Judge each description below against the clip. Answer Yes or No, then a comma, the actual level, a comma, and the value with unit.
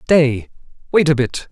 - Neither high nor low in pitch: Yes, medium, 145 Hz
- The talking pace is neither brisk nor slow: Yes, average, 160 wpm